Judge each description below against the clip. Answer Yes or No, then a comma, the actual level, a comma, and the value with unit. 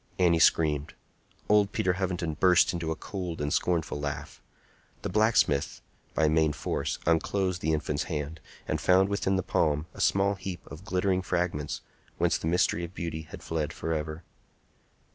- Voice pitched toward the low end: Yes, very low, 85 Hz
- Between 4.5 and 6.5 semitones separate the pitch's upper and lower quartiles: No, average, 3.2 semitones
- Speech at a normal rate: Yes, average, 160 wpm